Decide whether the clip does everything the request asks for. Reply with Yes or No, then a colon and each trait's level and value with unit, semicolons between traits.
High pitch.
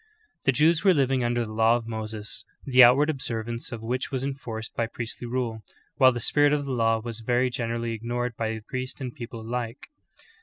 No: low, 120 Hz